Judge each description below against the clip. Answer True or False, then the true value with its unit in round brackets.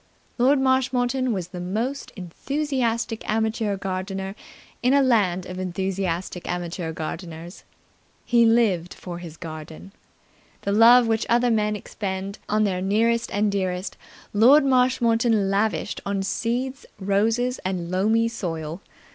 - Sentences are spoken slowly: True (125 wpm)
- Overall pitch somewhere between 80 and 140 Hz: False (205 Hz)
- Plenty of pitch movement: False (4.2 semitones)